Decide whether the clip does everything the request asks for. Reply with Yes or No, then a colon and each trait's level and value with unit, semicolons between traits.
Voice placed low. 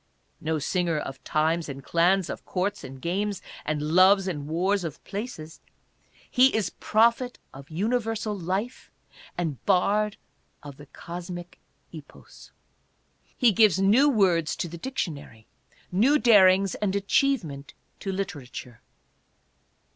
No: medium, 185 Hz